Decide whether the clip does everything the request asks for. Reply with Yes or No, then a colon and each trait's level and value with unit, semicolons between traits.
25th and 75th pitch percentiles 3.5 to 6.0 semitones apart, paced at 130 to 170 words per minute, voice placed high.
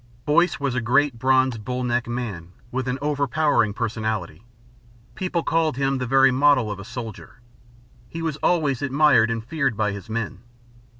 No: average, 4.1 semitones; average, 165 wpm; low, 125 Hz